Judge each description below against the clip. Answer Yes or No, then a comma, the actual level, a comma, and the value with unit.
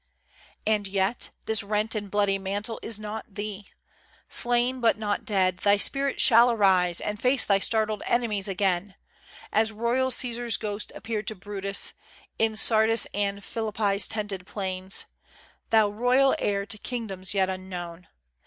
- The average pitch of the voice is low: No, high, 210 Hz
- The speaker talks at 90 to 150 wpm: Yes, average, 145 wpm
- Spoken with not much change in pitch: Yes, narrow, 2.3 semitones